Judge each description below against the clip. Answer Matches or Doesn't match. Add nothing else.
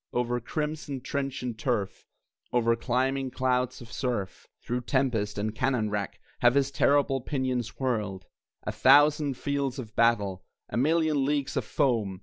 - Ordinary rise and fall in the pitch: Matches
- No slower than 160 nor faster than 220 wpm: Doesn't match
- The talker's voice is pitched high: Doesn't match